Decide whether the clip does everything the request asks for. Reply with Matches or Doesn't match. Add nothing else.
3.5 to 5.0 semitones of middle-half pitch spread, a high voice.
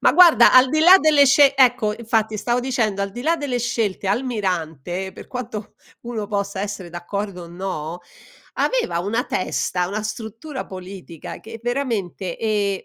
Matches